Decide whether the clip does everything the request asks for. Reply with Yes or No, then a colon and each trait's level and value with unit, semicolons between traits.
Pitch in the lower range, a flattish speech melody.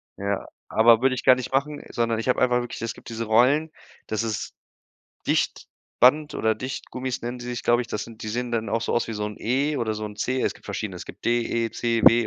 Yes: low, 120 Hz; narrow, 2.2 semitones